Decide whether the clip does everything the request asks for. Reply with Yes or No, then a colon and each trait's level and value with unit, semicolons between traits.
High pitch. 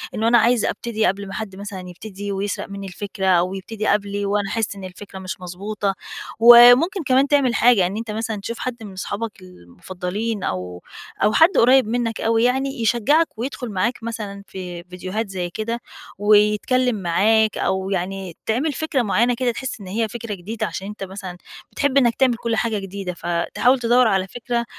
Yes: high, 210 Hz